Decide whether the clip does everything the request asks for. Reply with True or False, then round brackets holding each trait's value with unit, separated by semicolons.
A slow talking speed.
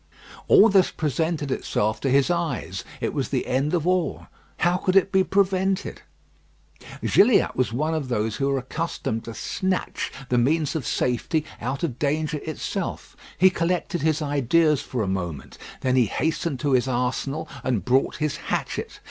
False (165 wpm)